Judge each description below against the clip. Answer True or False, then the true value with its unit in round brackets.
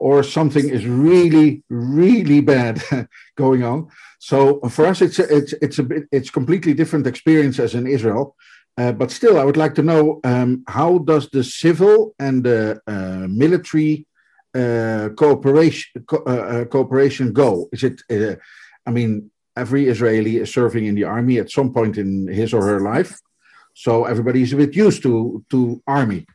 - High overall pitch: False (135 Hz)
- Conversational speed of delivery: True (170 wpm)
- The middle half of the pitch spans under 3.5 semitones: False (4.3 semitones)